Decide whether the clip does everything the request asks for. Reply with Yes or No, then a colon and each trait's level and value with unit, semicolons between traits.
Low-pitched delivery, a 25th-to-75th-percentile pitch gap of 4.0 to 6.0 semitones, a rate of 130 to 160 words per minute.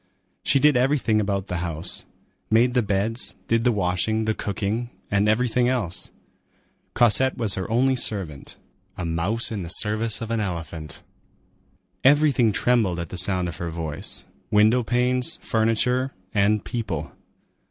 Yes: low, 110 Hz; average, 4.9 semitones; average, 140 wpm